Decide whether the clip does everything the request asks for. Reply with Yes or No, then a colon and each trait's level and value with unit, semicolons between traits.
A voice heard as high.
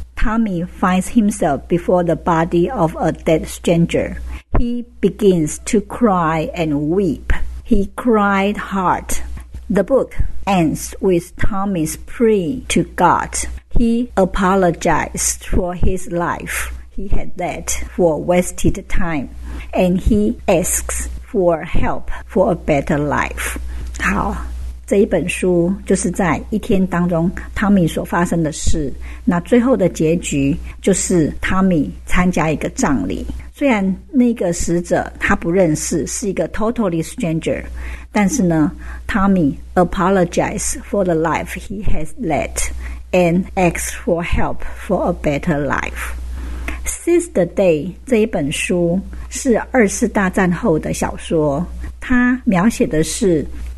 No: medium, 175 Hz